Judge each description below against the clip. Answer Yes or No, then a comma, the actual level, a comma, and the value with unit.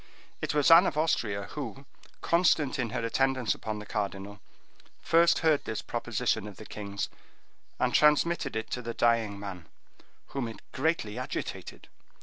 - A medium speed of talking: Yes, average, 150 wpm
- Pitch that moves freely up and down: Yes, wide, 6.0 semitones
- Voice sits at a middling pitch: No, low, 120 Hz